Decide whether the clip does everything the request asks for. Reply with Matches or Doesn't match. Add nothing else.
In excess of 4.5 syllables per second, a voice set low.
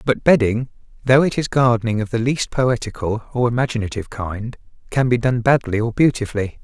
Matches